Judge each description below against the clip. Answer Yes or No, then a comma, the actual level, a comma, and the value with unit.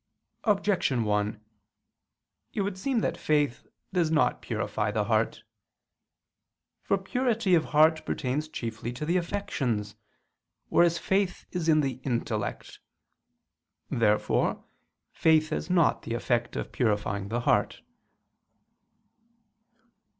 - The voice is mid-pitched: Yes, medium, 155 Hz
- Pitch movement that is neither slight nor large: No, wide, 7.3 semitones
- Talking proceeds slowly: Yes, slow, 115 wpm